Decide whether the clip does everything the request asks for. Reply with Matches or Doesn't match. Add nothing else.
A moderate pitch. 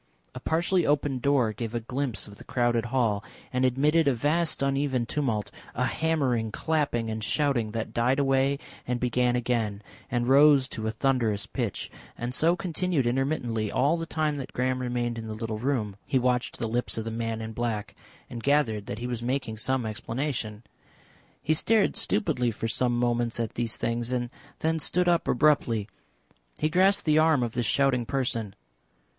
Doesn't match